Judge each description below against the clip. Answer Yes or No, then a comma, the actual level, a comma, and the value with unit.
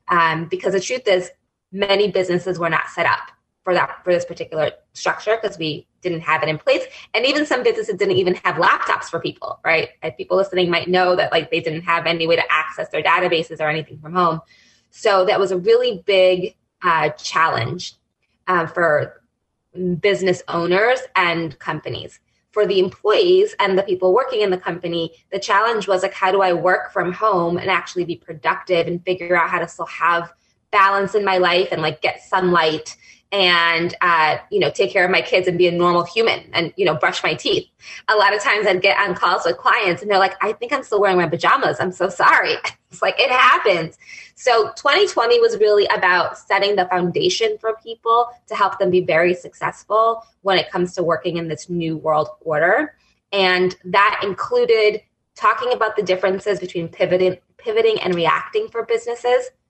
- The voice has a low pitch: No, medium, 185 Hz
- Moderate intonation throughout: Yes, average, 3.9 semitones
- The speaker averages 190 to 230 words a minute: Yes, average, 195 wpm